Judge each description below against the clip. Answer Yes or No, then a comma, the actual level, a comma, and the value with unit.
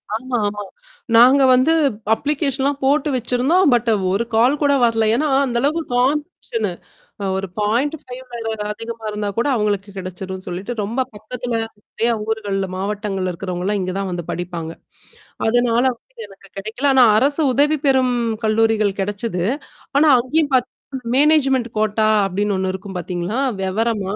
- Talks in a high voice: Yes, high, 225 Hz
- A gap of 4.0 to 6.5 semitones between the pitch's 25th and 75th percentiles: Yes, average, 4.9 semitones